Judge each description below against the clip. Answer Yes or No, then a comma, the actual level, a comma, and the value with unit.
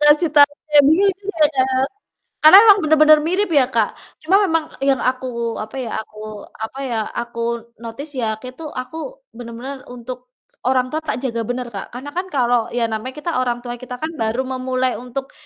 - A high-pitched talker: Yes, very high, 255 Hz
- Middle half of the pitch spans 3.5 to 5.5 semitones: Yes, average, 4.3 semitones